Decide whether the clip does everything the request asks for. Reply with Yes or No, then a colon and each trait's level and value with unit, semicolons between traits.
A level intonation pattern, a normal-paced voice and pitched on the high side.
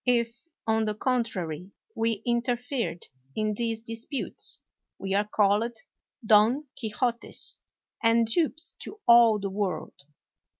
No: narrow, 2.3 semitones; slow, 115 wpm; high, 225 Hz